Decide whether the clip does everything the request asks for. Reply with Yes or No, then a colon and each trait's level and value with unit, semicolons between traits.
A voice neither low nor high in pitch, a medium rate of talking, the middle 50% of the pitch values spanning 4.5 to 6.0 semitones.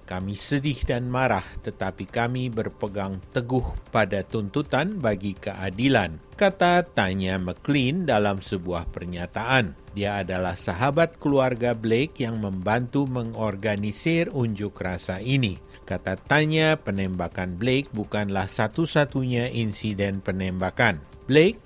No: low, 105 Hz; average, 105 wpm; average, 5.3 semitones